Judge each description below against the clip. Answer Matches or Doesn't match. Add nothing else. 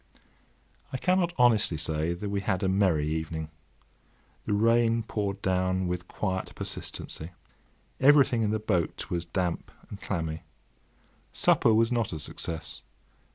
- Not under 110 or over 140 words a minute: Matches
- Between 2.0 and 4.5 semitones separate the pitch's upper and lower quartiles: Doesn't match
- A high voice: Doesn't match